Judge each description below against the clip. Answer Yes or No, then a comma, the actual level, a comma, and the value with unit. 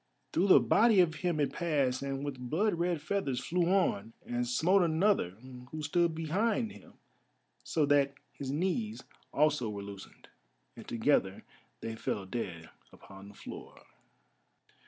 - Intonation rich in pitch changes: Yes, wide, 6.5 semitones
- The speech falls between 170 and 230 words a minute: No, average, 145 wpm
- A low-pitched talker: No, medium, 150 Hz